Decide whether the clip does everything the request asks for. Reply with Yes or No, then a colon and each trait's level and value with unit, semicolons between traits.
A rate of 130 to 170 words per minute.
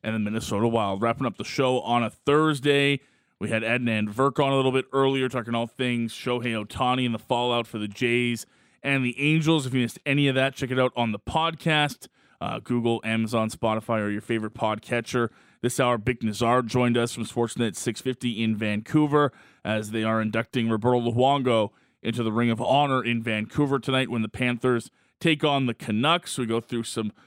No: average, 200 wpm